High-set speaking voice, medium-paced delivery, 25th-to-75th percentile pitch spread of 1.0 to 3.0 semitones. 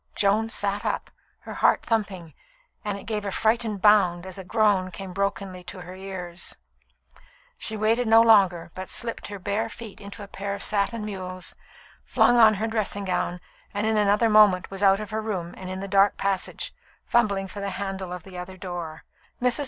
Yes: high, 200 Hz; average, 190 wpm; narrow, 2.4 semitones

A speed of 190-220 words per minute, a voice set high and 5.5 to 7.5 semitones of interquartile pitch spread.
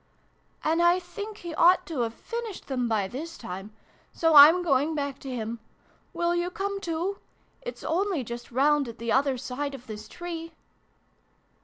No: average, 175 wpm; very high, 300 Hz; wide, 5.8 semitones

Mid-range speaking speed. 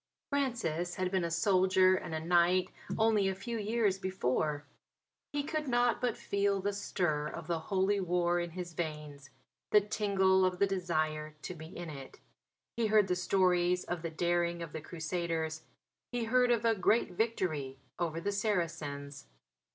Yes: average, 165 wpm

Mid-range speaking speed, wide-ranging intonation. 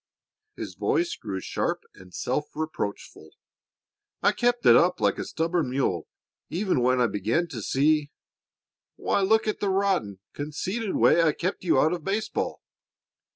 Yes: average, 155 wpm; wide, 7.2 semitones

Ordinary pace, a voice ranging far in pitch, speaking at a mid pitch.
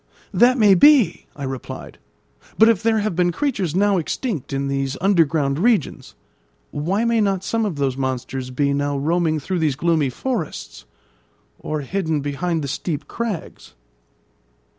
Yes: average, 150 wpm; wide, 6.4 semitones; medium, 165 Hz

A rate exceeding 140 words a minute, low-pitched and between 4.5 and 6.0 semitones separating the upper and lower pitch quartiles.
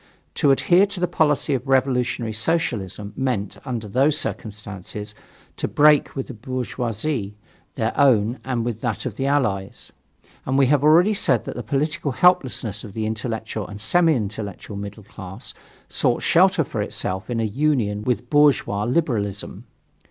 Yes: average, 150 wpm; low, 120 Hz; average, 5.2 semitones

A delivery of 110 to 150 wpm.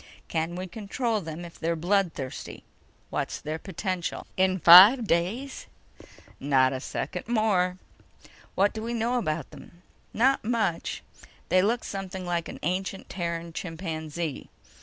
Yes: slow, 135 wpm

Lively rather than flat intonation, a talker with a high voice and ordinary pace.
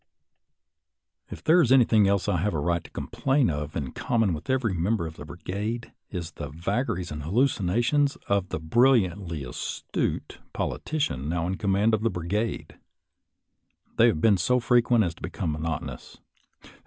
No: wide, 6.0 semitones; low, 100 Hz; average, 175 wpm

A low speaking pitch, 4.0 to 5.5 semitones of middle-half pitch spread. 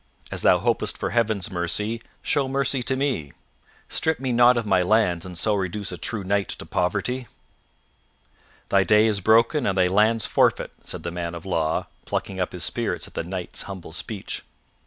Yes: low, 100 Hz; average, 4.3 semitones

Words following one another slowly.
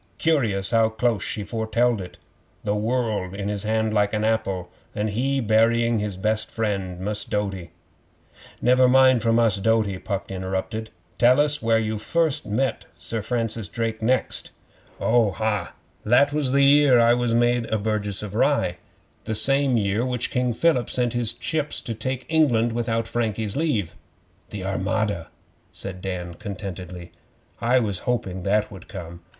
No: average, 155 wpm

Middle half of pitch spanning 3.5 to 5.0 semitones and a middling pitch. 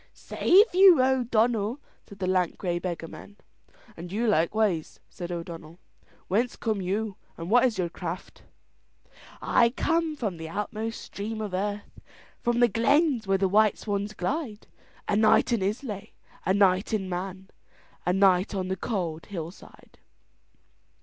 No: average, 3.8 semitones; high, 205 Hz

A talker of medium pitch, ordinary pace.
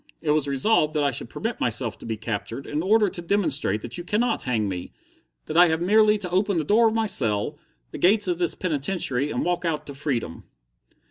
No: medium, 160 Hz; fast, 220 wpm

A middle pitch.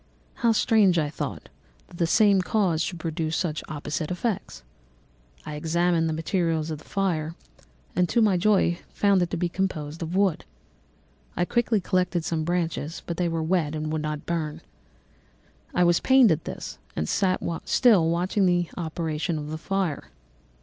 Yes: medium, 170 Hz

